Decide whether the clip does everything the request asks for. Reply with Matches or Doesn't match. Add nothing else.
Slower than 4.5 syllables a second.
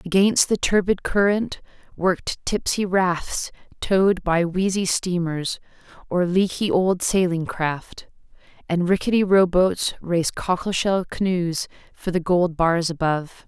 Matches